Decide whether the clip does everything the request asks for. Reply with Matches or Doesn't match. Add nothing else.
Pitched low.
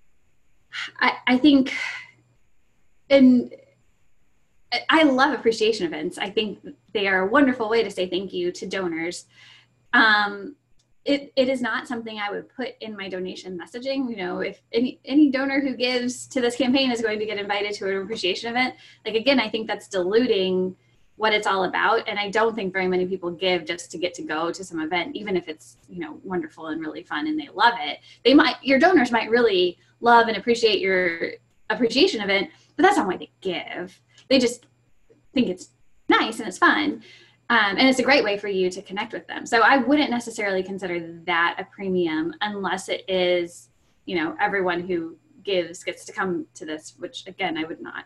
Doesn't match